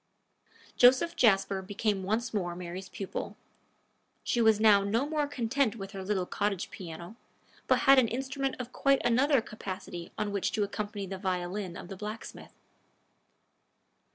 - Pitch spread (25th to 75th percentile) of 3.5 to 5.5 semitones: Yes, average, 4.1 semitones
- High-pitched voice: Yes, high, 210 Hz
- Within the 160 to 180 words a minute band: No, average, 150 wpm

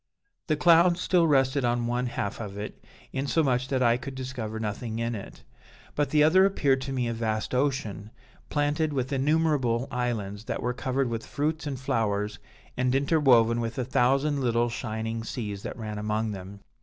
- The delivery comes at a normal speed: Yes, average, 175 wpm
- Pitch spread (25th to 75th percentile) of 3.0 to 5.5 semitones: Yes, average, 3.8 semitones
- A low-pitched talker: Yes, low, 125 Hz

